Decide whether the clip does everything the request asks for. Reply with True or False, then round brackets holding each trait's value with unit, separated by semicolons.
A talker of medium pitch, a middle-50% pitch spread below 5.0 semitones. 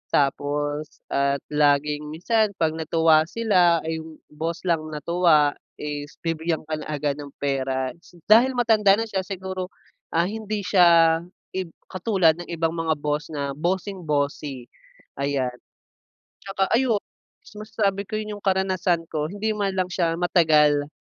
True (165 Hz; 4.4 semitones)